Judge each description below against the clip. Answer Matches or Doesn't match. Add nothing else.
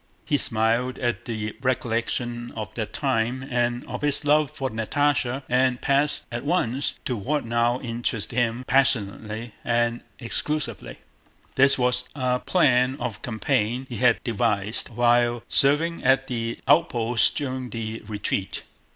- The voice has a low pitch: Matches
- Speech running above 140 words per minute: Doesn't match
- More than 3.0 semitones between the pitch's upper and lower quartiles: Doesn't match